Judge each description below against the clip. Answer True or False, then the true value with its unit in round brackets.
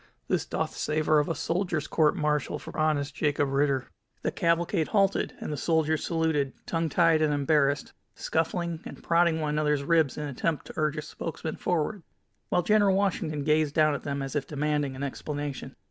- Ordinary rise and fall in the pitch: False (2.2 semitones)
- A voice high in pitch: False (155 Hz)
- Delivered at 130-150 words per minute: False (185 wpm)